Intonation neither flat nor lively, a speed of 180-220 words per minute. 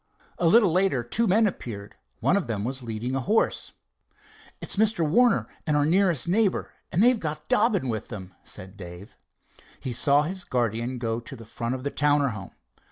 No: wide, 8.2 semitones; average, 190 wpm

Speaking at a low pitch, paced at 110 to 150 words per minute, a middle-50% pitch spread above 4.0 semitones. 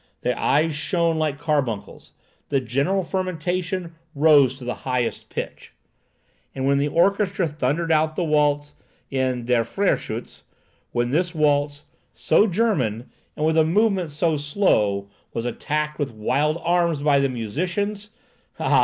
No: medium, 150 Hz; slow, 135 wpm; average, 4.4 semitones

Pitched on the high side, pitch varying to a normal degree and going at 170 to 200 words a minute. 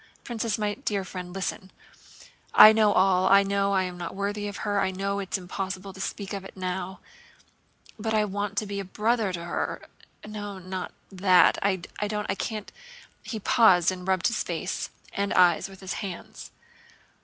No: high, 195 Hz; narrow, 1.8 semitones; average, 185 wpm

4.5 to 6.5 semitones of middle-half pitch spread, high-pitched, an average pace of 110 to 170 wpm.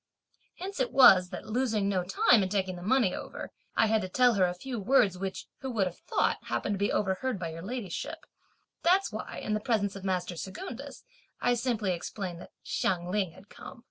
No: average, 4.8 semitones; high, 200 Hz; fast, 205 wpm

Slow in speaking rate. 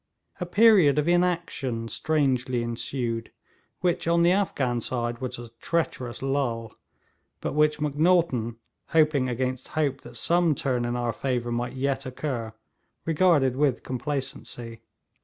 Yes: slow, 130 wpm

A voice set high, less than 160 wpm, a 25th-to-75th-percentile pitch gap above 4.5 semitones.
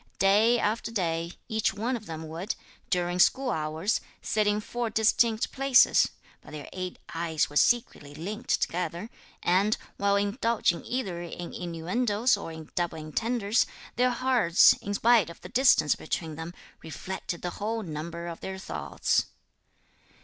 Yes: high, 195 Hz; average, 150 wpm; average, 5.2 semitones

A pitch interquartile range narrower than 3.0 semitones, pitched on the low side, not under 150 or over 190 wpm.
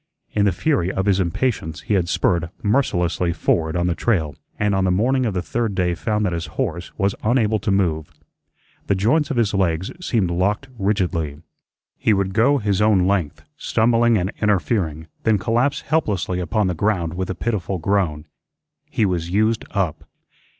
No: average, 3.8 semitones; very low, 95 Hz; average, 180 wpm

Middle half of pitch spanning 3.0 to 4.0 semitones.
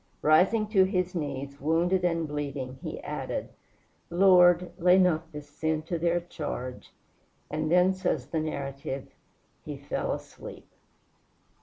Yes: average, 3.5 semitones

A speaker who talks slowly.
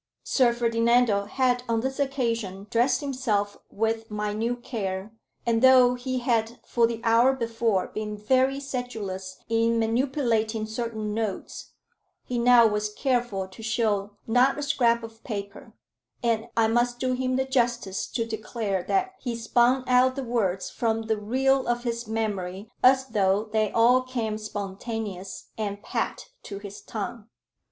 No: average, 150 wpm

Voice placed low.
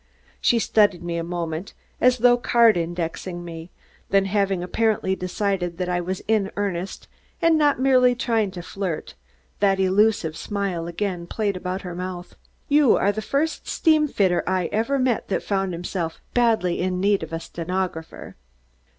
No: high, 190 Hz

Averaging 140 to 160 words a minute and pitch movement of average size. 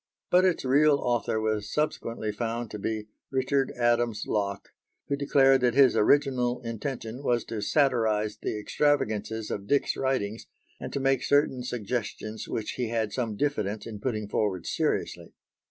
Yes: average, 155 wpm; average, 3.9 semitones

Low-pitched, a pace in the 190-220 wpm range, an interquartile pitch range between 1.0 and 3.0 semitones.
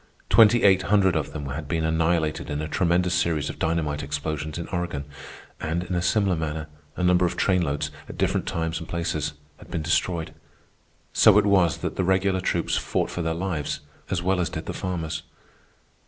Yes: very low, 85 Hz; average, 195 wpm; average, 2.7 semitones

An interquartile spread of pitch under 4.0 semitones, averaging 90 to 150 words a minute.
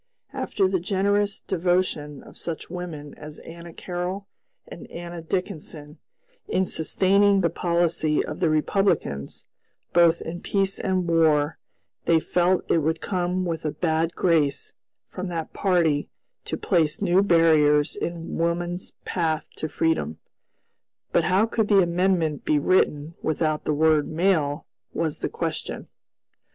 Yes: average, 2.9 semitones; slow, 135 wpm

